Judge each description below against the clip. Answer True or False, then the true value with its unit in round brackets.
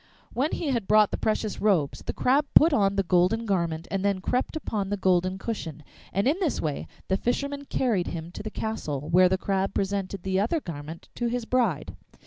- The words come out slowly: False (205 wpm)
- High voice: True (195 Hz)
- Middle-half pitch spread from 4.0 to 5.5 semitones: True (4.6 semitones)